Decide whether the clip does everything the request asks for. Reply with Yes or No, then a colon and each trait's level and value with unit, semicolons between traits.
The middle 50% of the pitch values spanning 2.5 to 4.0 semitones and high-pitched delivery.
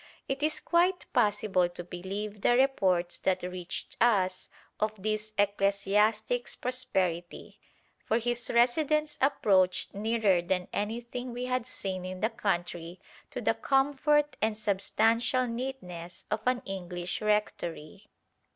No: average, 4.8 semitones; high, 210 Hz